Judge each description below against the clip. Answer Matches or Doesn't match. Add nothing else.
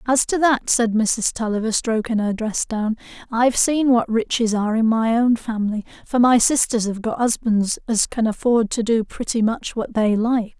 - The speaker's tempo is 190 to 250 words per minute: Matches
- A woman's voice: Matches